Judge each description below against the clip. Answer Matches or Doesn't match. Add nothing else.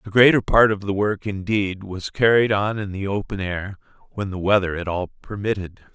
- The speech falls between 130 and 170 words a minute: Doesn't match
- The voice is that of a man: Matches